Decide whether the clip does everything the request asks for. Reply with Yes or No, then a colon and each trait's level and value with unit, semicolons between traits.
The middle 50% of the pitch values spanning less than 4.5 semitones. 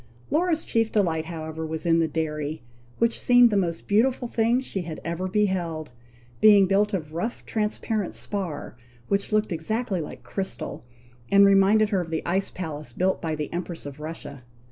No: average, 4.8 semitones